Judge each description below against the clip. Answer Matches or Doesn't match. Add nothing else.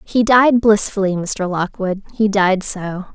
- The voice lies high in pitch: Matches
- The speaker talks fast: Doesn't match